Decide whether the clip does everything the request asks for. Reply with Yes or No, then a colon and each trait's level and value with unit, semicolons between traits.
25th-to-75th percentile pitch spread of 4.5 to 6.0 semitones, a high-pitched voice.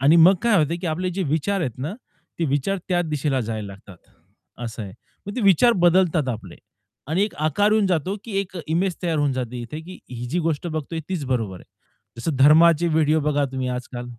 No: wide, 5.5 semitones; medium, 155 Hz